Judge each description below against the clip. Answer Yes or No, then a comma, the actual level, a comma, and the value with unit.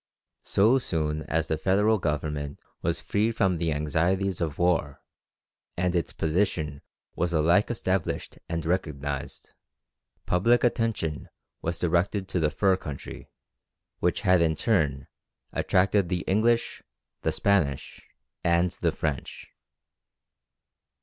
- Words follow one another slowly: Yes, slow, 115 wpm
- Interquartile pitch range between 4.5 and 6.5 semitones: No, average, 4.1 semitones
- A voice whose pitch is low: Yes, very low, 85 Hz